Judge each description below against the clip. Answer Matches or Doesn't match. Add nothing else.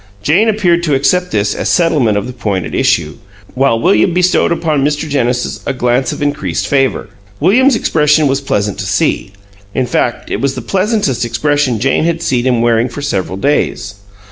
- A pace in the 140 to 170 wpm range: Doesn't match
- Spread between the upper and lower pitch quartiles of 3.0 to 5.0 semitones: Doesn't match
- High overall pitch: Doesn't match